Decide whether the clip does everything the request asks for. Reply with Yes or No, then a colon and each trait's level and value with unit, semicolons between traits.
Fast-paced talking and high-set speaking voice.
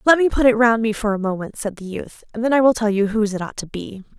Yes: fast, 330 wpm; high, 220 Hz